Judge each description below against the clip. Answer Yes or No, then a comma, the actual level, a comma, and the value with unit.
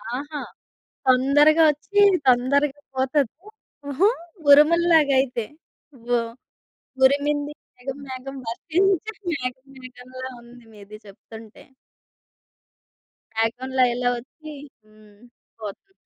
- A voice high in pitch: Yes, very high, 260 Hz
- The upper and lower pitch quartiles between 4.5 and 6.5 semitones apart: No, average, 3.3 semitones